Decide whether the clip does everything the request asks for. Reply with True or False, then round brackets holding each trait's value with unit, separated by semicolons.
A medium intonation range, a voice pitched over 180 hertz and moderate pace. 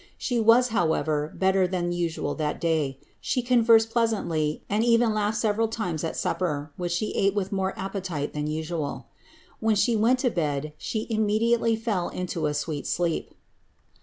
False (5.8 semitones; 190 Hz; 165 wpm)